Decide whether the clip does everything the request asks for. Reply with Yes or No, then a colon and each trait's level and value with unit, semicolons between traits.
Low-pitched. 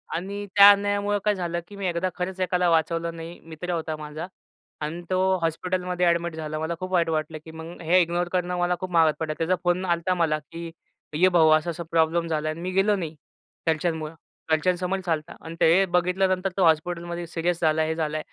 No: medium, 170 Hz